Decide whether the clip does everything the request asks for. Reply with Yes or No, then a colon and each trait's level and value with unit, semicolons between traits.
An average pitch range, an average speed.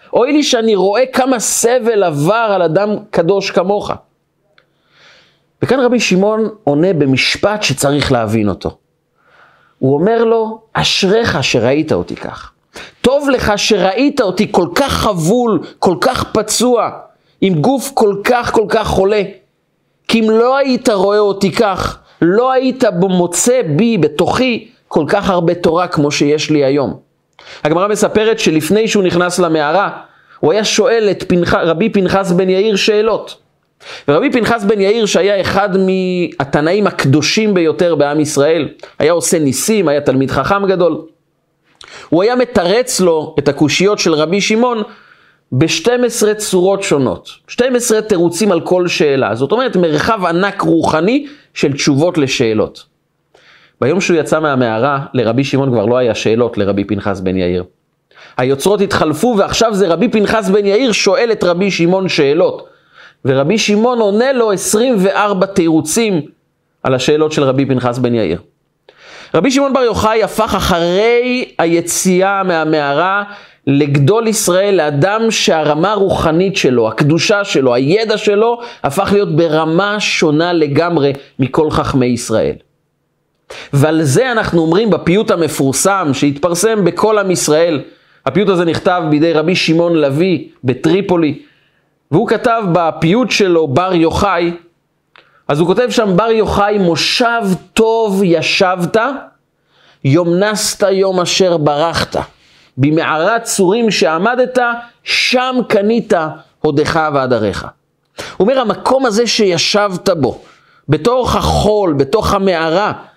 No: wide, 5.8 semitones; average, 130 wpm